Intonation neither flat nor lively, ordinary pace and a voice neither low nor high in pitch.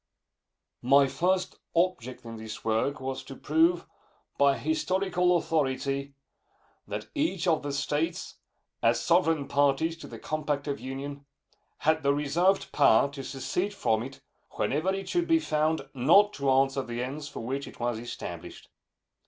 Yes: average, 4.1 semitones; average, 150 wpm; medium, 145 Hz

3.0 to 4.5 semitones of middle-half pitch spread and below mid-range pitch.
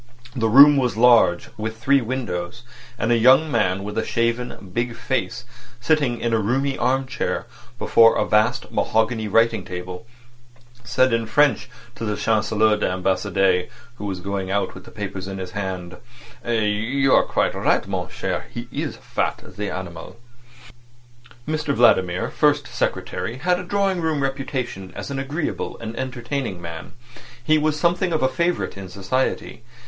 No: average, 5.2 semitones; low, 115 Hz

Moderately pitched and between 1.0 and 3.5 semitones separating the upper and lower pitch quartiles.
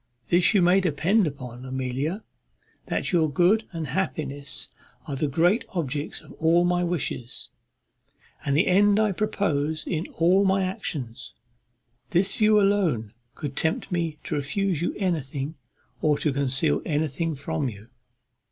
No: medium, 160 Hz; average, 4.8 semitones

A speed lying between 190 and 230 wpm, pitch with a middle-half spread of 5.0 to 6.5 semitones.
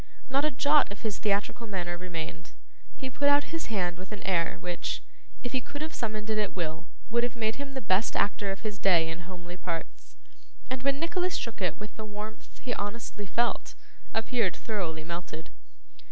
Yes: average, 195 wpm; wide, 5.4 semitones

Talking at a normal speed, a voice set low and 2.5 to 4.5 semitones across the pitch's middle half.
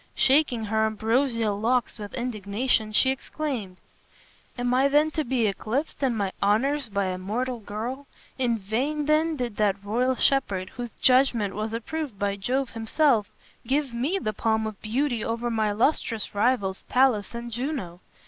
No: average, 160 wpm; high, 235 Hz; average, 3.9 semitones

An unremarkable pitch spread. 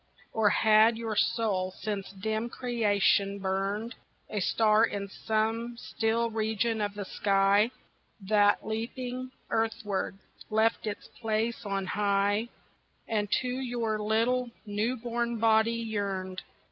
No: narrow, 2.1 semitones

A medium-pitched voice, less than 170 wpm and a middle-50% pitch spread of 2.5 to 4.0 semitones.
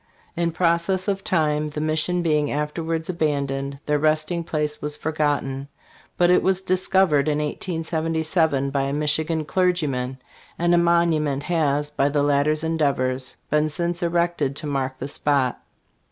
Yes: medium, 155 Hz; average, 150 wpm; average, 2.9 semitones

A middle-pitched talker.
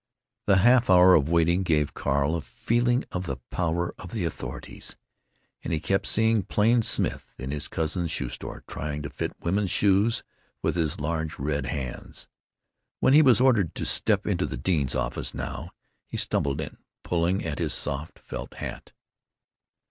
No: very low, 85 Hz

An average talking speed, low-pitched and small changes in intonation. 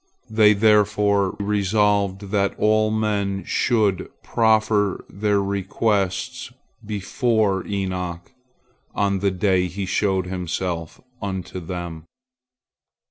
No: slow, 90 wpm; low, 100 Hz; narrow, 2.0 semitones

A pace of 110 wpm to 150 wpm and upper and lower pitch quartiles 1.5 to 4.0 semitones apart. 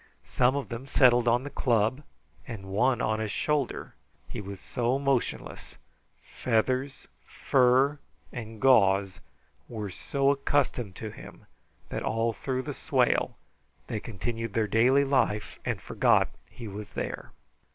Yes: slow, 135 wpm; average, 3.4 semitones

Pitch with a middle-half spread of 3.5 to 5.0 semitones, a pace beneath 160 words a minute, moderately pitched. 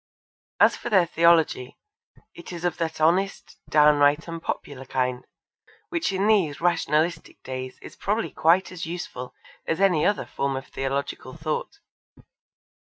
Yes: average, 3.9 semitones; average, 140 wpm; medium, 165 Hz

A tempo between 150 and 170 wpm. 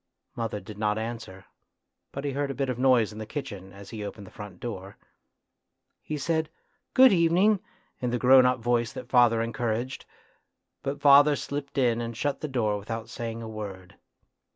No: average, 190 wpm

